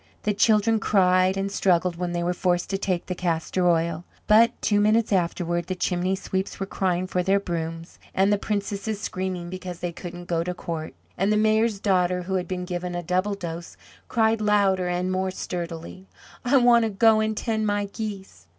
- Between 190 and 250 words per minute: Yes, average, 195 wpm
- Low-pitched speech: No, medium, 185 Hz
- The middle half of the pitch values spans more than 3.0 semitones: No, narrow, 2.6 semitones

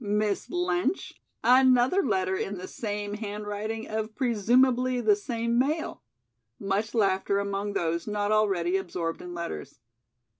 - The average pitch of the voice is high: Yes, high, 210 Hz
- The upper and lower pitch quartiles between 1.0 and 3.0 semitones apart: No, average, 3.4 semitones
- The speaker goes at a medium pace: No, slow, 125 wpm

